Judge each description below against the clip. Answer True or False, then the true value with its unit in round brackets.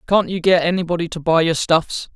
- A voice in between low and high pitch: True (170 Hz)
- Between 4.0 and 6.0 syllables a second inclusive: True (5.6 syllables/s)